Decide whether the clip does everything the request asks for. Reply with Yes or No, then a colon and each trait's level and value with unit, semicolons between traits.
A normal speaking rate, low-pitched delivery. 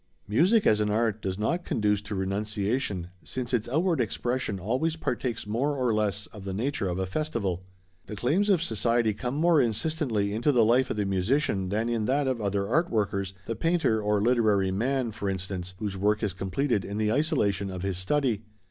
Yes: average, 195 wpm; low, 110 Hz